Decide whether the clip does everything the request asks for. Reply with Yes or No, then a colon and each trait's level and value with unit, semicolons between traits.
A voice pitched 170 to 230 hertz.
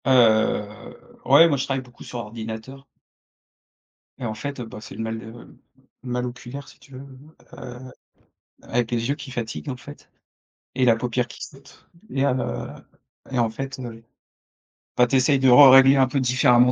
No: low, 125 Hz